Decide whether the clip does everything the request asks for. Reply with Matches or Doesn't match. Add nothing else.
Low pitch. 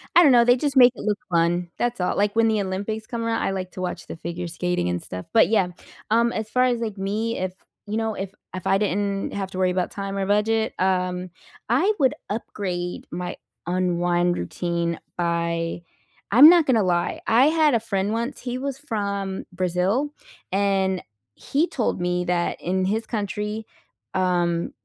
Doesn't match